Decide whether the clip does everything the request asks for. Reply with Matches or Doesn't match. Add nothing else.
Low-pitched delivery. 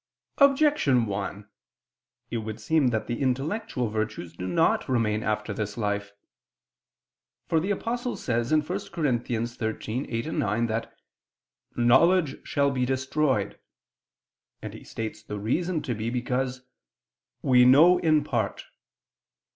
Matches